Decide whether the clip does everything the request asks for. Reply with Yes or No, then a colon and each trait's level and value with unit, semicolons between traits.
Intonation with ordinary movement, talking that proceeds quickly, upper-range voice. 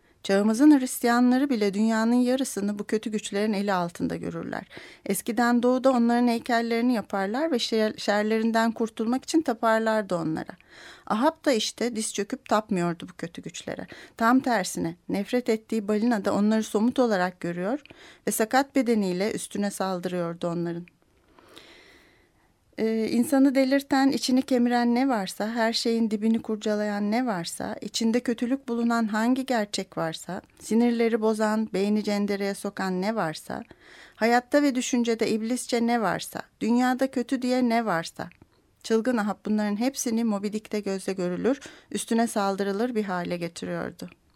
No: average, 3.2 semitones; average, 130 wpm; high, 225 Hz